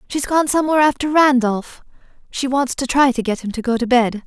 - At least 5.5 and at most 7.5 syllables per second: Yes, 5.9 syllables/s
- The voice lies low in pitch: No, very high, 260 Hz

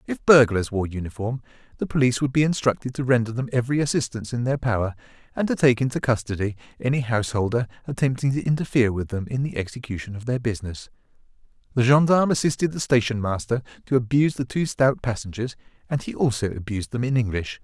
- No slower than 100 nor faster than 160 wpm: No, average, 185 wpm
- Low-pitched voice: Yes, low, 120 Hz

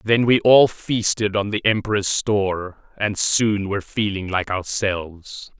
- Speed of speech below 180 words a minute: Yes, average, 150 wpm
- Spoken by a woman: No, male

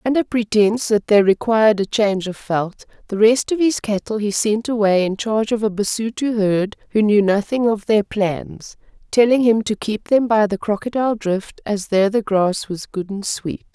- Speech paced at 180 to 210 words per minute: Yes, average, 200 wpm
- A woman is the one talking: Yes, female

